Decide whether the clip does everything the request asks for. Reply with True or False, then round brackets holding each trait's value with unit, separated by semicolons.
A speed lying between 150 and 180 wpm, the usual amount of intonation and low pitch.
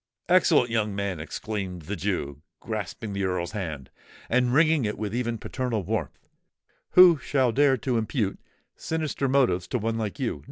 True (160 wpm; 4.8 semitones; 110 Hz)